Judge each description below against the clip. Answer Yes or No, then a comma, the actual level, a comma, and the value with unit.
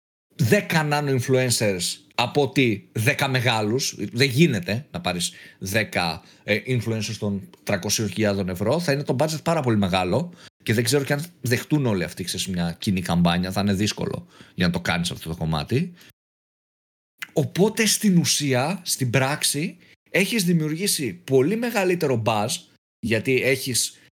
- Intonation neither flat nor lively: No, wide, 7.1 semitones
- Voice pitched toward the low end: Yes, low, 130 Hz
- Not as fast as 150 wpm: Yes, average, 140 wpm